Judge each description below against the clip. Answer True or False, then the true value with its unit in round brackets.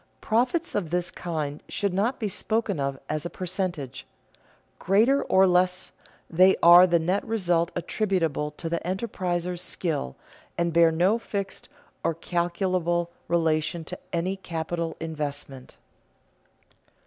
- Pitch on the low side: False (175 Hz)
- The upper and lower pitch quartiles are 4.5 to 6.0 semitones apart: False (2.7 semitones)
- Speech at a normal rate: False (125 wpm)